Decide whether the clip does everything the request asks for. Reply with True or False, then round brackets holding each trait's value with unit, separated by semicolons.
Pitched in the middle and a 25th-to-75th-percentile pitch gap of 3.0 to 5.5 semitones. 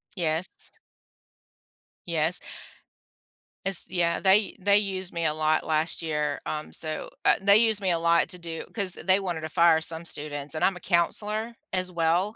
True (170 Hz; 3.3 semitones)